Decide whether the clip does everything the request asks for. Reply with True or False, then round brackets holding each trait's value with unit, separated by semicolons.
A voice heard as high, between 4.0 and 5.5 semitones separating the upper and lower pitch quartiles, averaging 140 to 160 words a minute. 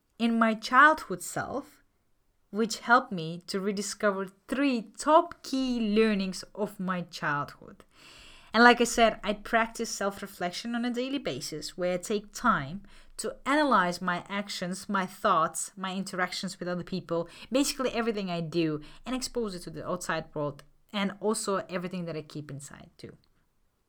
True (195 Hz; 4.5 semitones; 155 wpm)